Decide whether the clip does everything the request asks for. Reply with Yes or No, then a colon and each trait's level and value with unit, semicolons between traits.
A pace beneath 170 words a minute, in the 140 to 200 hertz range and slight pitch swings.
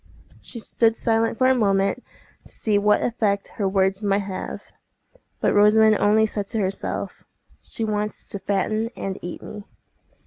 No: average, 160 wpm; high, 210 Hz; narrow, 1.9 semitones